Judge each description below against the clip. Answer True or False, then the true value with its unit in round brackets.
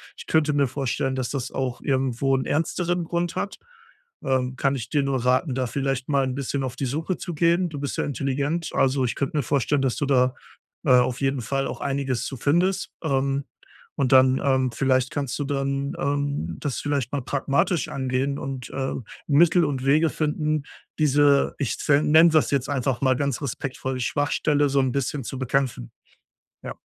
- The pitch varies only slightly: True (1.9 semitones)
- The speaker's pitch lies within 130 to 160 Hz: True (140 Hz)